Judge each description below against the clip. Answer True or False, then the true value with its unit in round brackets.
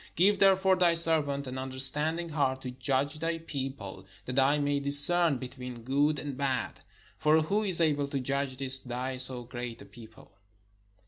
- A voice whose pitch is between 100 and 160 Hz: True (140 Hz)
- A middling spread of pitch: True (3.4 semitones)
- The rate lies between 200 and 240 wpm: False (170 wpm)